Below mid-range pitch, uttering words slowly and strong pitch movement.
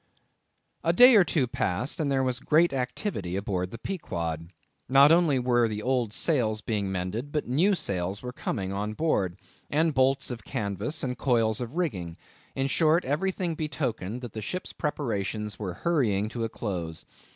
No: low, 125 Hz; average, 170 wpm; wide, 6.6 semitones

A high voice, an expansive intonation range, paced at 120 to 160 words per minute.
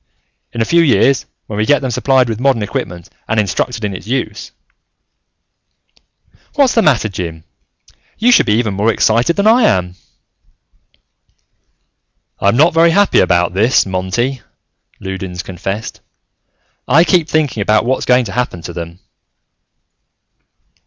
No: low, 115 Hz; wide, 6.4 semitones; average, 145 wpm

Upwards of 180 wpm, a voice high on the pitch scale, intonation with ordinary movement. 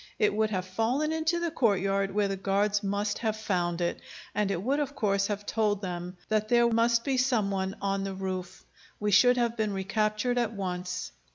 Yes: average, 200 wpm; high, 205 Hz; average, 3.1 semitones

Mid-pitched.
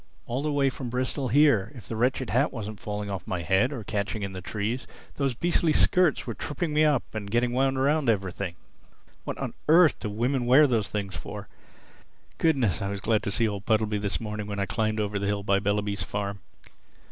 No: low, 110 Hz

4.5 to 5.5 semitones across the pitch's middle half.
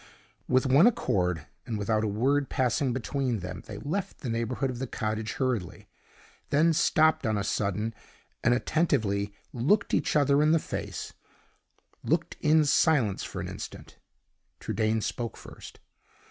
Yes: average, 5.1 semitones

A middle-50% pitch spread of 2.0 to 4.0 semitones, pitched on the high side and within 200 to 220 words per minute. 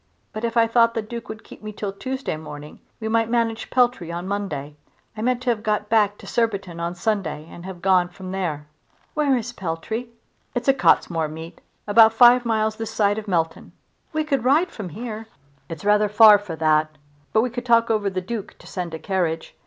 No: average, 4.6 semitones; high, 210 Hz; fast, 205 wpm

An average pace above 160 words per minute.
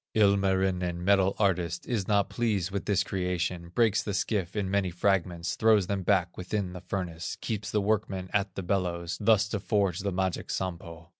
Yes: average, 175 wpm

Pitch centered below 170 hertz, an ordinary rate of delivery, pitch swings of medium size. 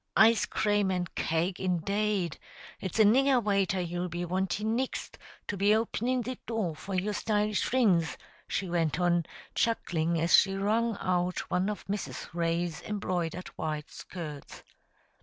No: high, 190 Hz; average, 145 wpm; average, 3.5 semitones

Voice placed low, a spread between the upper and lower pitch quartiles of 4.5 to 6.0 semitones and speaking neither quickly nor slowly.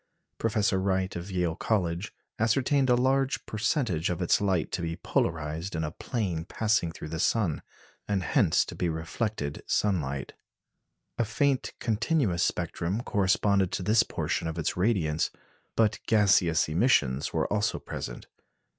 Yes: very low, 95 Hz; average, 5.0 semitones; average, 145 wpm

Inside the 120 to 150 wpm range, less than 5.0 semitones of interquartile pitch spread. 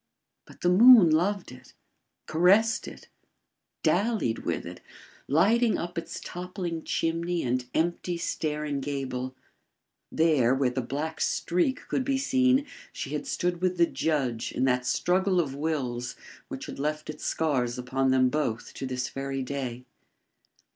No: average, 145 wpm; average, 5.3 semitones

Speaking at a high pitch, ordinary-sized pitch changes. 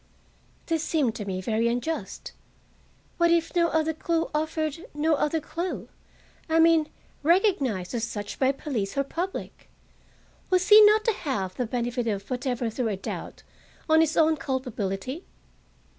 No: very high, 295 Hz; wide, 5.8 semitones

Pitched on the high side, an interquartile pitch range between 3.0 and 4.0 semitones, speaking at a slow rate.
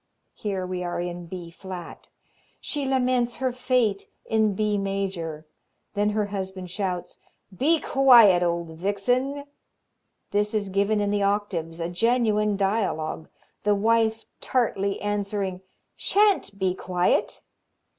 Yes: high, 200 Hz; average, 3.5 semitones; slow, 125 wpm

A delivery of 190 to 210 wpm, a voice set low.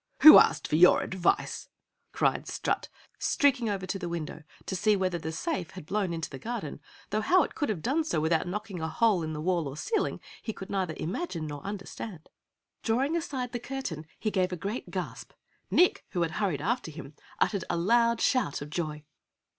No: average, 200 wpm; high, 190 Hz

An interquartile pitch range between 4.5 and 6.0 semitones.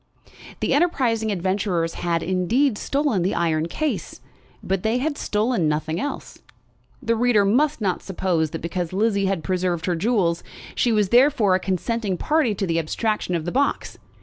Yes: average, 5.3 semitones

